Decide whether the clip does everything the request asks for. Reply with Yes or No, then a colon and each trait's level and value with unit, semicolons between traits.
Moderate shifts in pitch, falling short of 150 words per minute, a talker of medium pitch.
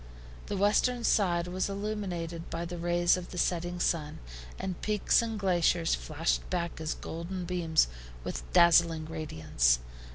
No: narrow, 2.3 semitones; average, 140 wpm; medium, 175 Hz